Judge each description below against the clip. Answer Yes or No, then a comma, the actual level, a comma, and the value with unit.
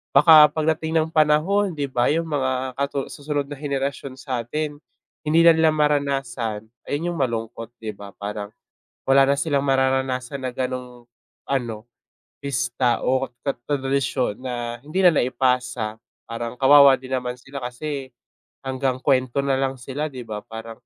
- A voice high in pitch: No, low, 135 Hz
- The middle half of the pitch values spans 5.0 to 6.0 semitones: No, average, 2.9 semitones